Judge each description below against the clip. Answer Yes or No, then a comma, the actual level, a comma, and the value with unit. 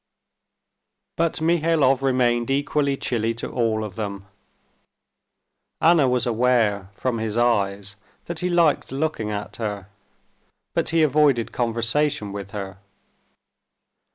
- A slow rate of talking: Yes, slow, 115 wpm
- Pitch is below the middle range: Yes, low, 120 Hz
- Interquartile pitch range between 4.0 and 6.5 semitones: Yes, wide, 5.6 semitones